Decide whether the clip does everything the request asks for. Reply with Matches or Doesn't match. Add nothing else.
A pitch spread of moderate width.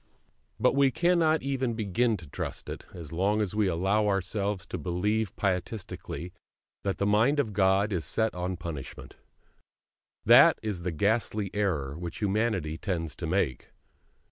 Matches